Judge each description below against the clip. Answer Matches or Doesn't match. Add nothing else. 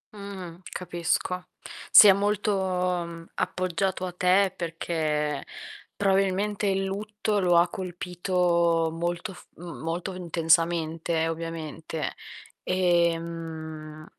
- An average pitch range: Doesn't match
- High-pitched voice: Doesn't match